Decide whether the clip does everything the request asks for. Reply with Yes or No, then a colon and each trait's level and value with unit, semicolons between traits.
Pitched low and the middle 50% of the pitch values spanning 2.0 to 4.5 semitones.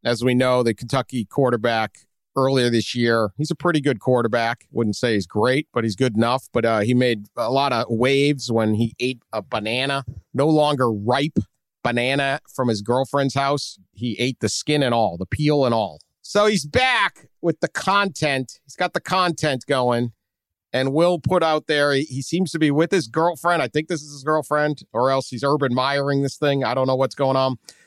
Yes: low, 130 Hz; average, 4.0 semitones